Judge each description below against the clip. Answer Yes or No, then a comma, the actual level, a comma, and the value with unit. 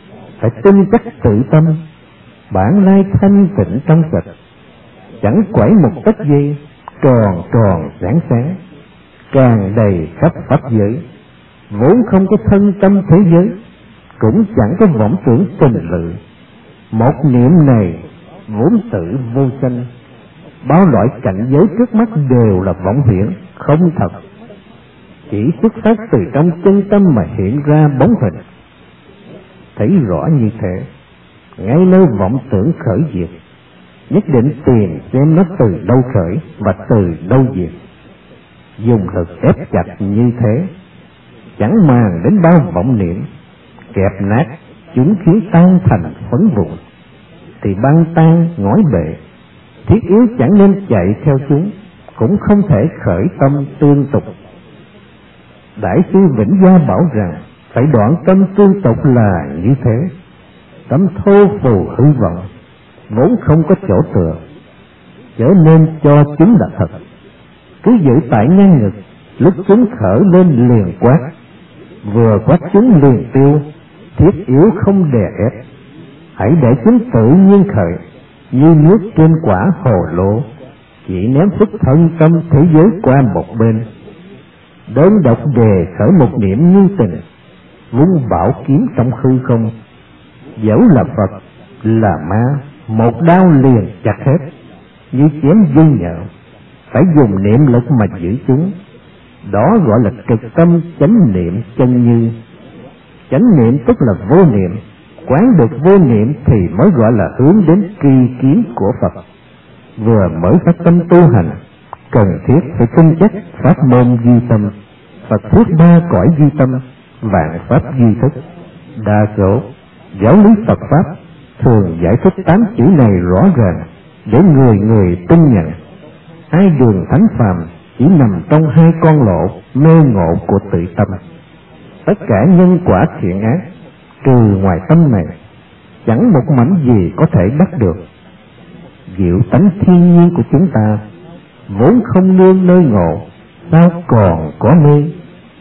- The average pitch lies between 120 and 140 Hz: Yes, low, 135 Hz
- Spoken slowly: Yes, slow, 150 wpm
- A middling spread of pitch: No, wide, 8.2 semitones